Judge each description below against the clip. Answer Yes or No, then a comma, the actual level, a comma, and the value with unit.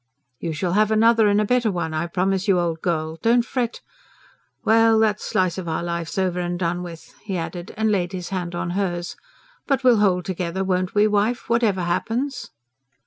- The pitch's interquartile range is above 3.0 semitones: Yes, average, 3.9 semitones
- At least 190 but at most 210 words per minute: Yes, average, 195 wpm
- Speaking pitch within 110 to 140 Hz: No, medium, 185 Hz